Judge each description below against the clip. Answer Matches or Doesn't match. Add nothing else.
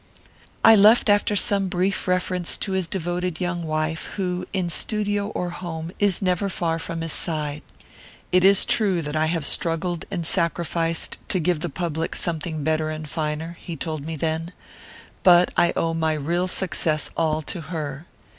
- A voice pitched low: Doesn't match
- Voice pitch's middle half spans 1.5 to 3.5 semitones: Matches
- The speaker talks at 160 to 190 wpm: Matches